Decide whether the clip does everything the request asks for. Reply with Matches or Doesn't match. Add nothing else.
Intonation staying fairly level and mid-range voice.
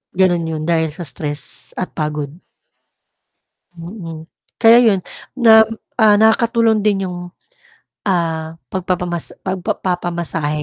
Doesn't match